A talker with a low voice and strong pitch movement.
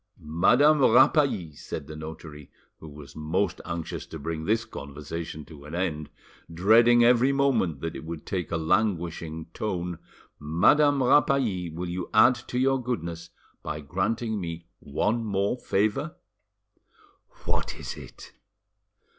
Yes: very low, 90 Hz; wide, 6.7 semitones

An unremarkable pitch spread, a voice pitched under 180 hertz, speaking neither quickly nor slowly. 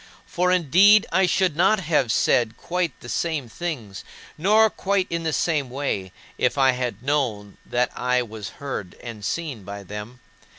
No: wide, 6.9 semitones; medium, 140 Hz; average, 165 wpm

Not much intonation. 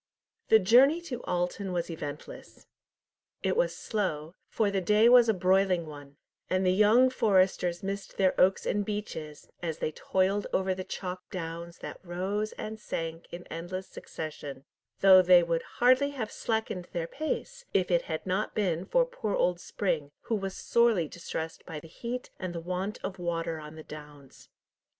No: average, 4.0 semitones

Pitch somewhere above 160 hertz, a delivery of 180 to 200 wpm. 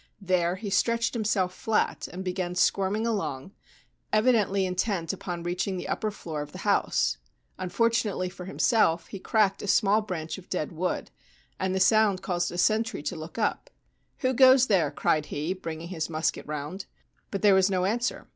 Yes: high, 190 Hz; average, 185 wpm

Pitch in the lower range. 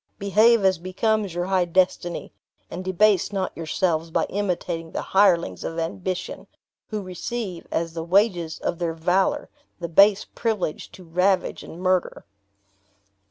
No: medium, 185 Hz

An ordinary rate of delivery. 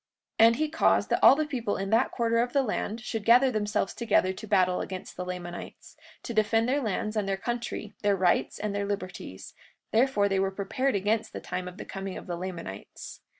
No: fast, 215 wpm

